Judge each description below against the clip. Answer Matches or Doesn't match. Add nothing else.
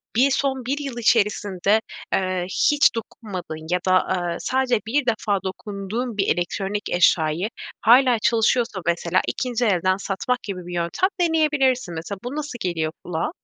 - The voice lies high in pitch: Matches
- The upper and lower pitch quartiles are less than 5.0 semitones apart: Doesn't match